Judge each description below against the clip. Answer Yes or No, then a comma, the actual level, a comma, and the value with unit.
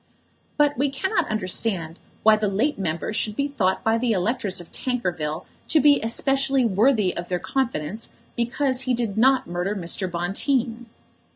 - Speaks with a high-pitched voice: Yes, high, 225 Hz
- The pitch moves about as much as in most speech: No, wide, 6.2 semitones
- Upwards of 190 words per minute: No, average, 160 wpm